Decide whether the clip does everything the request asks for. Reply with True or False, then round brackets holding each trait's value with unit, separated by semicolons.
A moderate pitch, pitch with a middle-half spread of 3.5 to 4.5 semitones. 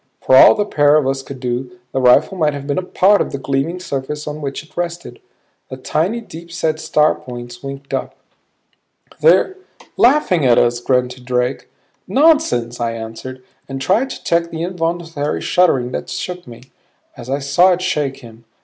False (145 Hz; 5.2 semitones)